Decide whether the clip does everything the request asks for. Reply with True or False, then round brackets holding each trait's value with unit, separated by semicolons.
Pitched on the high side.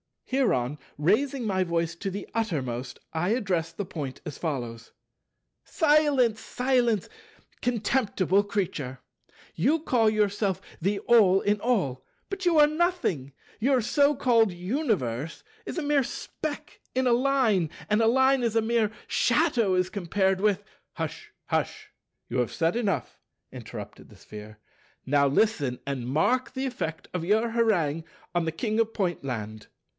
True (205 Hz)